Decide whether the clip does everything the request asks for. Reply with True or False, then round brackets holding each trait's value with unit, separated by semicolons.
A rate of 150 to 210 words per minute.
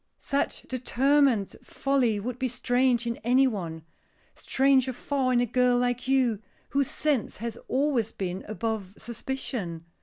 False (140 wpm)